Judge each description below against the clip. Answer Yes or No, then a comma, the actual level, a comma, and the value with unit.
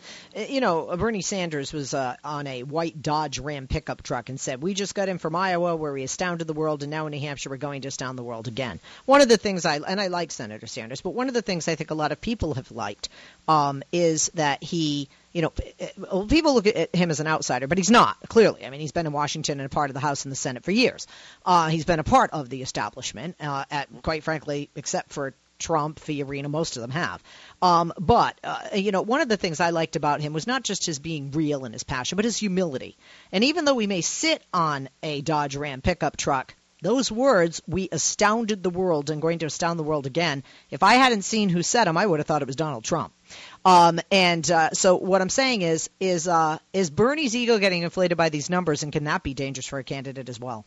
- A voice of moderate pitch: Yes, medium, 160 Hz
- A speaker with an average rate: No, fast, 250 wpm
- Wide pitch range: No, average, 4.4 semitones